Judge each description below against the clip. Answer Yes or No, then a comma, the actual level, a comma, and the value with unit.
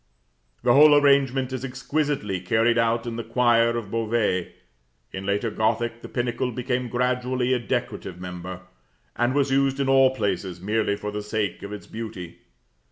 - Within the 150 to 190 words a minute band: Yes, average, 165 wpm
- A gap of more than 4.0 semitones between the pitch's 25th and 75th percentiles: No, average, 3.6 semitones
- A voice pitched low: Yes, low, 115 Hz